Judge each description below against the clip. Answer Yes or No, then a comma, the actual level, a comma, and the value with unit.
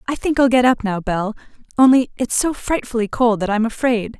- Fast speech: Yes, fast, 215 wpm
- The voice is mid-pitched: No, high, 235 Hz